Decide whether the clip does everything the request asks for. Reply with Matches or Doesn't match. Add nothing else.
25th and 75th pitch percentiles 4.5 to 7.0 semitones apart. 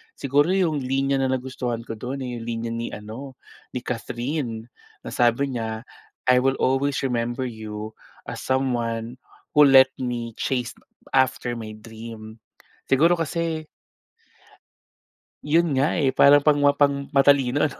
Doesn't match